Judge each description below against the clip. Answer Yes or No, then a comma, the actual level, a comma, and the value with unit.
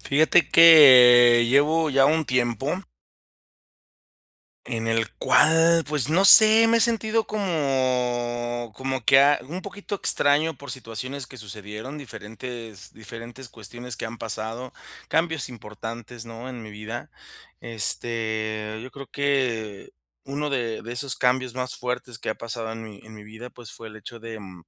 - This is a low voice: Yes, low, 125 Hz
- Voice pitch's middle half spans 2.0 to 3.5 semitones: No, average, 4.0 semitones